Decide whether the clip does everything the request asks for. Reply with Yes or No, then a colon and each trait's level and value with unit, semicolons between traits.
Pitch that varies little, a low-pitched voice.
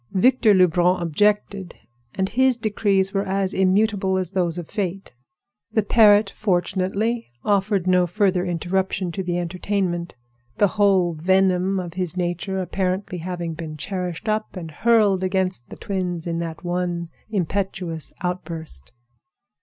No: narrow, 2.3 semitones; medium, 185 Hz